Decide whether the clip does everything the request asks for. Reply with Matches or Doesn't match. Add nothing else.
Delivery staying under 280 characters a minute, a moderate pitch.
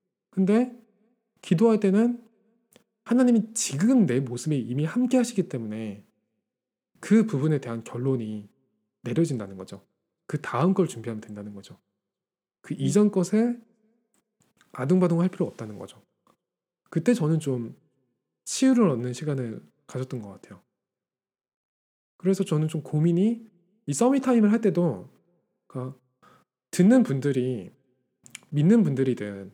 Matches